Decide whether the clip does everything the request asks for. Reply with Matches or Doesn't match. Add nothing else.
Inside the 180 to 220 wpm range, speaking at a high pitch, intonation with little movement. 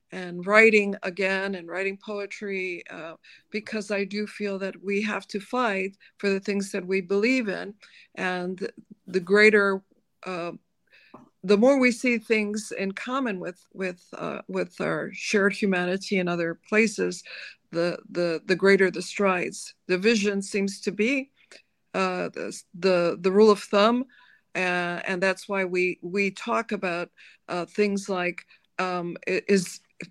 Doesn't match